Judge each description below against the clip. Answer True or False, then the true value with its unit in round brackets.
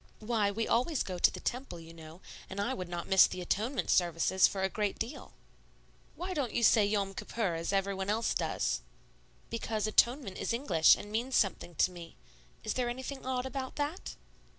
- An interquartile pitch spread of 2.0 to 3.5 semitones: False (5.0 semitones)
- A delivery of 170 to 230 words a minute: True (190 wpm)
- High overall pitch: True (210 Hz)